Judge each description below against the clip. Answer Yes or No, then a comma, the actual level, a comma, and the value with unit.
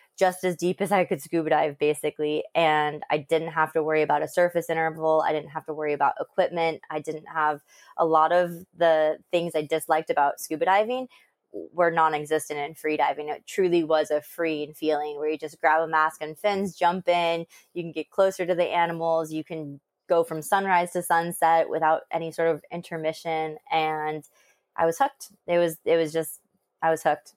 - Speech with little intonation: Yes, narrow, 1.8 semitones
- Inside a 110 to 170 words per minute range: No, average, 200 wpm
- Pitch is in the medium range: Yes, medium, 160 Hz